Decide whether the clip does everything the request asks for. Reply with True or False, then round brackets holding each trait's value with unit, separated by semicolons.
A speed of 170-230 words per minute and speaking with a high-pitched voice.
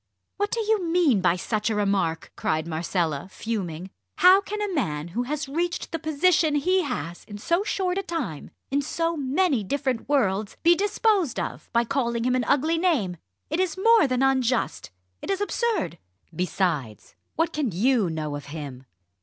True (175 wpm; 265 Hz)